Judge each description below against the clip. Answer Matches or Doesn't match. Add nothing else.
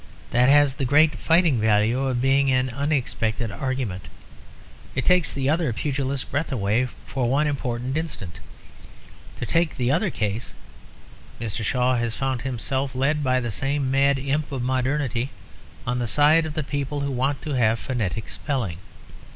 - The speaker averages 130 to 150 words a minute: Doesn't match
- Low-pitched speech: Matches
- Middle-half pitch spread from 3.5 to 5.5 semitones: Doesn't match